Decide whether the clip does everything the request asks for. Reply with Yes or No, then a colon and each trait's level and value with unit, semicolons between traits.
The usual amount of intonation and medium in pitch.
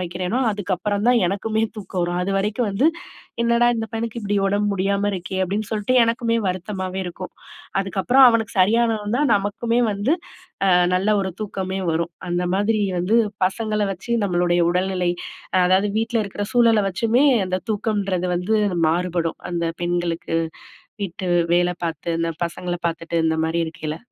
No: average, 3.6 semitones; high, 195 Hz